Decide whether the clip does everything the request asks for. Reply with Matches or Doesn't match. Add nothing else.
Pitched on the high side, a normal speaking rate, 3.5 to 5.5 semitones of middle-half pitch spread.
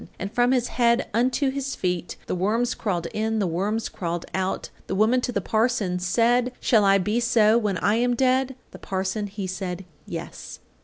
Matches